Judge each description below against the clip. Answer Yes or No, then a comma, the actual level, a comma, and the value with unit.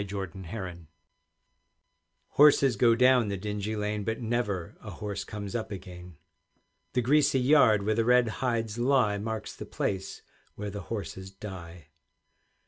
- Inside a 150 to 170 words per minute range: No, slow, 135 wpm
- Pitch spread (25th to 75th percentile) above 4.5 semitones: No, average, 3.5 semitones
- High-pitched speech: No, low, 105 Hz